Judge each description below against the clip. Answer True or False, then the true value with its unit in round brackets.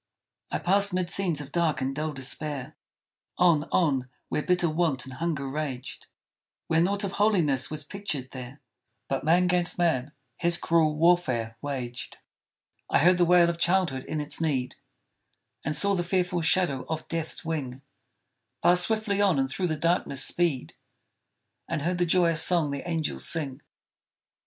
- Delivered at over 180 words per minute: False (160 wpm)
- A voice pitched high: False (160 Hz)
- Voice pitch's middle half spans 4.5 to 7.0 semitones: False (4.1 semitones)